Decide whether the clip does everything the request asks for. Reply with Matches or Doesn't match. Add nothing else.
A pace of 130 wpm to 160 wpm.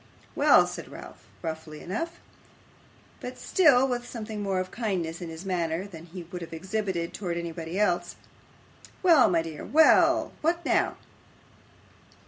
Matches